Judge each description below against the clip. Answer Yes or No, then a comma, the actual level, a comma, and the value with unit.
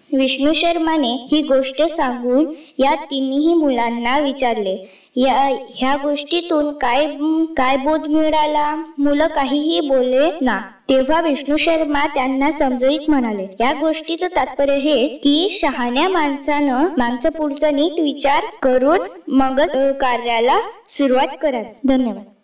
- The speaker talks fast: No, average, 110 wpm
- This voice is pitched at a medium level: No, very high, 285 Hz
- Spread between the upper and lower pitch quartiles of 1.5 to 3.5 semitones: Yes, average, 2.7 semitones